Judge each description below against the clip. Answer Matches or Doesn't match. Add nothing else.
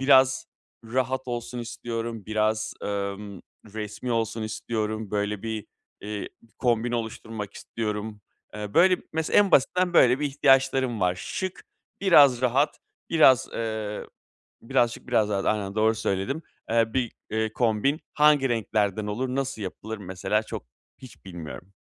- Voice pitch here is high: Doesn't match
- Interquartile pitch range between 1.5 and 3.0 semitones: Doesn't match